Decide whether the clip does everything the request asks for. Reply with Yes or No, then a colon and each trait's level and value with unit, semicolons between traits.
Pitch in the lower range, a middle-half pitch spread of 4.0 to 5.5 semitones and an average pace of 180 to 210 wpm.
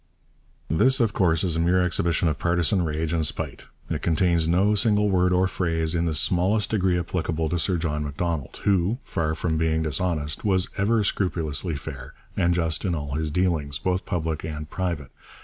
No: very low, 85 Hz; narrow, 2.6 semitones; average, 185 wpm